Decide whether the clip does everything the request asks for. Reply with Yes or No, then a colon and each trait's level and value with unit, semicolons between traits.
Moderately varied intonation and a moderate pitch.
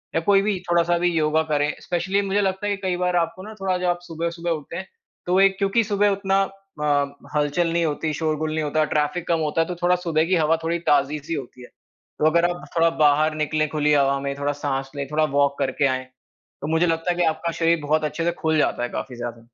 Yes: average, 3.0 semitones; medium, 160 Hz